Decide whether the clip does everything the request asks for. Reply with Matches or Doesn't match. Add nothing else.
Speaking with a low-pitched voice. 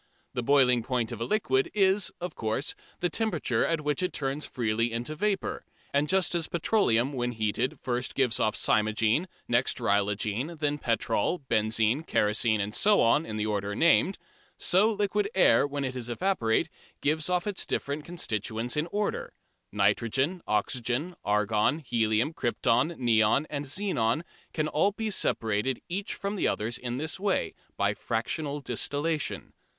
Matches